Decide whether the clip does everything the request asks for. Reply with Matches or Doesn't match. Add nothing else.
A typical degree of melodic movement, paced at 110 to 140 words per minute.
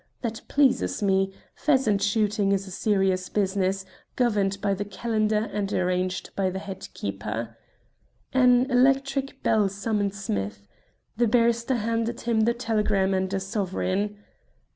Matches